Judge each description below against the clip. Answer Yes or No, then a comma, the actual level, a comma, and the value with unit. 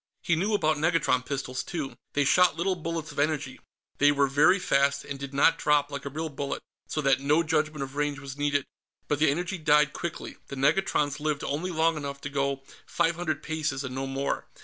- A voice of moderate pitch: Yes, medium, 145 Hz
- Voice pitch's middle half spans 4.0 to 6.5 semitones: No, narrow, 2.4 semitones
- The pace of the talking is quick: Yes, fast, 210 wpm